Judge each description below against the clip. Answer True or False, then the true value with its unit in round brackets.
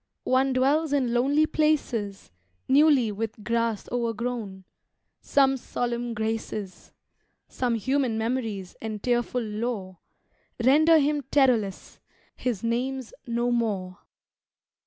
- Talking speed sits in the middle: False (100 wpm)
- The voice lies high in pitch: True (240 Hz)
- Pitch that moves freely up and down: False (3.4 semitones)